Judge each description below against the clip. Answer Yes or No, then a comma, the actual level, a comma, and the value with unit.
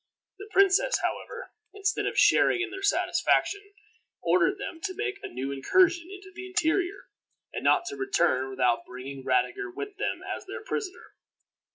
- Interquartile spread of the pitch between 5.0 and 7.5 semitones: No, average, 3.1 semitones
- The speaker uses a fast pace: No, average, 160 wpm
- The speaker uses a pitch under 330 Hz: No, very high, 375 Hz